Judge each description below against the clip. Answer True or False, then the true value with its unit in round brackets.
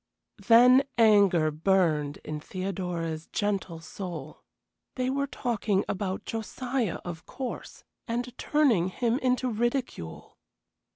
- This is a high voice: True (200 Hz)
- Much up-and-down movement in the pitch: True (6.5 semitones)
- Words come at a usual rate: False (105 wpm)